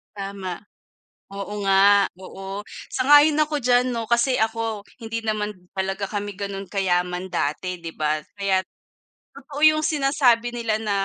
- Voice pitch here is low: No, high, 205 Hz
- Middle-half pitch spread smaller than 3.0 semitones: No, average, 3.9 semitones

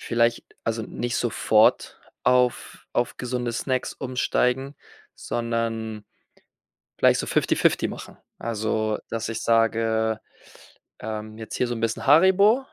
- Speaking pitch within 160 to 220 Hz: No, low, 115 Hz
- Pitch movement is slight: Yes, narrow, 2.0 semitones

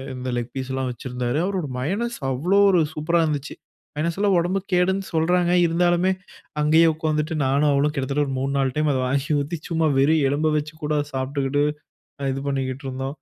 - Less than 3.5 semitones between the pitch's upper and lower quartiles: No, average, 4.0 semitones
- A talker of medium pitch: Yes, medium, 150 Hz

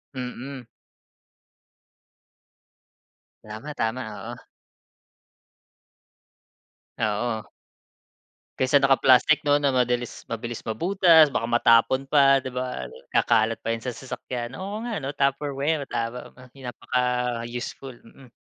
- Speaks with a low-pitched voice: Yes, low, 125 Hz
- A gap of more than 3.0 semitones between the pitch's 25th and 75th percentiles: No, narrow, 2.6 semitones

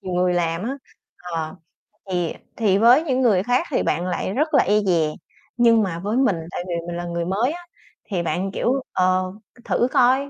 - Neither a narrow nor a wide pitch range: No, wide, 5.7 semitones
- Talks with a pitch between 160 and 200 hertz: Yes, high, 195 Hz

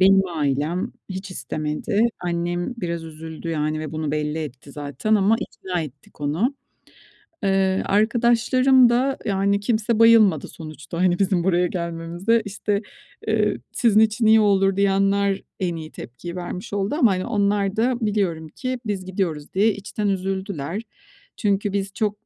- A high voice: Yes, high, 195 Hz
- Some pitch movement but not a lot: Yes, average, 4.1 semitones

